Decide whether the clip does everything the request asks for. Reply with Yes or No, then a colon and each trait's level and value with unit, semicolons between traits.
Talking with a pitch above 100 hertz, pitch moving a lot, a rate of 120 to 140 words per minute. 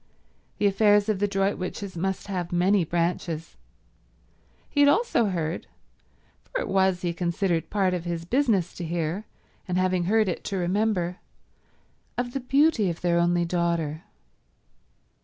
No: medium, 185 Hz; average, 3.1 semitones; slow, 135 wpm